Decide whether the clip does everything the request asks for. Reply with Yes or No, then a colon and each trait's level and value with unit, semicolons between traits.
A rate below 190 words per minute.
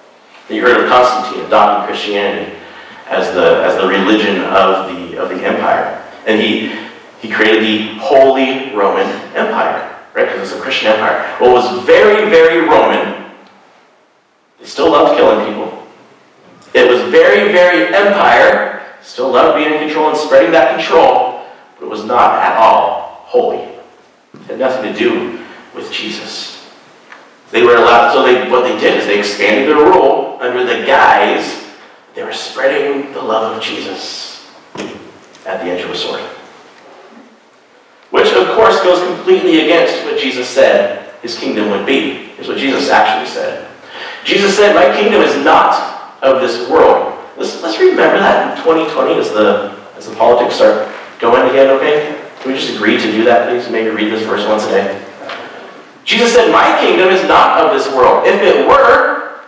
Yes: average, 170 wpm